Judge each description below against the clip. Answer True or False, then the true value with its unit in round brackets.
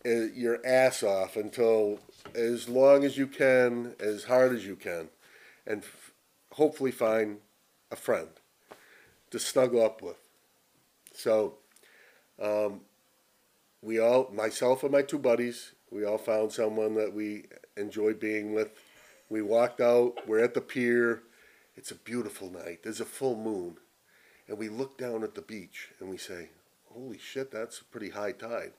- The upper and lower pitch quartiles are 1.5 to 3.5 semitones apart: True (3.0 semitones)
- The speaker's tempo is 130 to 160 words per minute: True (155 wpm)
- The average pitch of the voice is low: True (115 Hz)